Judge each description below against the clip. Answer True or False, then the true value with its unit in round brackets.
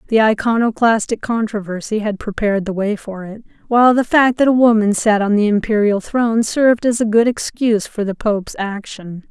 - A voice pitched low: False (220 Hz)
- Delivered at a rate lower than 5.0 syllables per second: False (5.4 syllables/s)